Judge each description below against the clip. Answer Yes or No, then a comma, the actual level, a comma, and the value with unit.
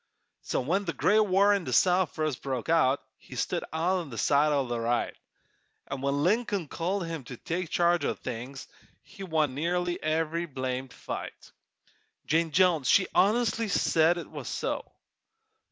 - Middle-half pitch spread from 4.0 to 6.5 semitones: Yes, average, 4.8 semitones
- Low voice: No, medium, 165 Hz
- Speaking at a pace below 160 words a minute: No, average, 165 wpm